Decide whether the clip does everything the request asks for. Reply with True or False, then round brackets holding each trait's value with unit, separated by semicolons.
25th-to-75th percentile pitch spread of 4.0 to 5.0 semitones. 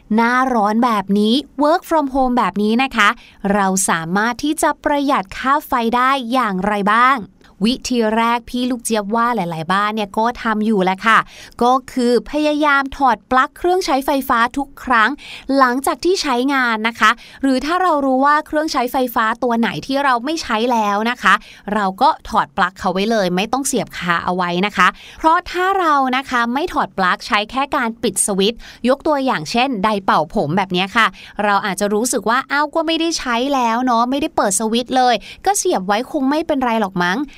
True (4.7 semitones)